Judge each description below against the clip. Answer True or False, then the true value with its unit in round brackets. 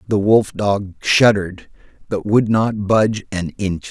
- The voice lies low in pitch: True (100 Hz)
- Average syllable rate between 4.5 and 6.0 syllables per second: False (4.0 syllables/s)